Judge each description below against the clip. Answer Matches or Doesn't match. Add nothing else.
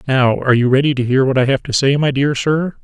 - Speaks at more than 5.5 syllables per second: Matches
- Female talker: Doesn't match